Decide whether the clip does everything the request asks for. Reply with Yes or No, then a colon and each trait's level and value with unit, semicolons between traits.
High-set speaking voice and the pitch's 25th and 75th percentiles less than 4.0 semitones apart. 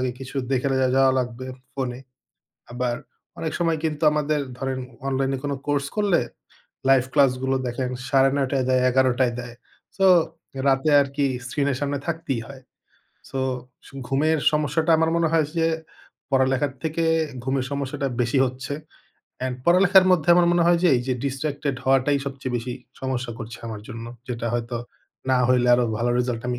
No: low, 135 Hz; narrow, 2.6 semitones